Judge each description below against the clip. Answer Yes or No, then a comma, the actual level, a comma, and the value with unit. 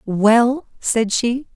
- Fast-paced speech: No, slow, 115 wpm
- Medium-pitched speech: No, high, 235 Hz